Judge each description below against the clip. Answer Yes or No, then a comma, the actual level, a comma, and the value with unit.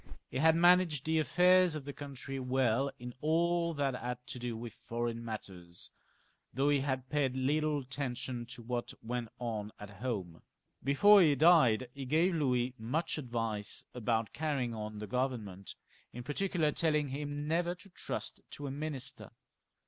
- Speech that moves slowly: No, average, 165 wpm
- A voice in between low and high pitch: No, low, 130 Hz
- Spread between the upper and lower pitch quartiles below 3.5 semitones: No, average, 4.4 semitones